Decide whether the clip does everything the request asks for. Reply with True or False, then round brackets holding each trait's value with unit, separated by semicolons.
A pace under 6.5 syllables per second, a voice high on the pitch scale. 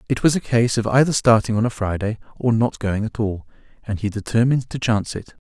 False (6.0 syllables/s; 115 Hz)